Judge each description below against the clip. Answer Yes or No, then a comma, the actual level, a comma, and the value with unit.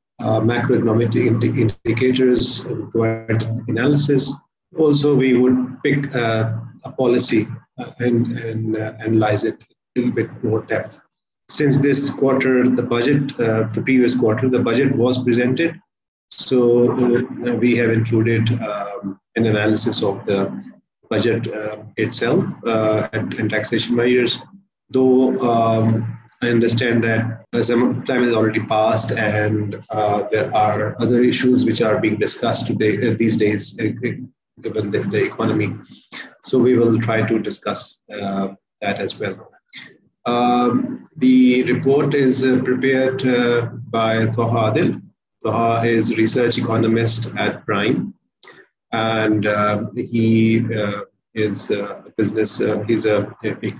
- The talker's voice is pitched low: Yes, low, 115 Hz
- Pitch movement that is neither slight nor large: No, narrow, 2.1 semitones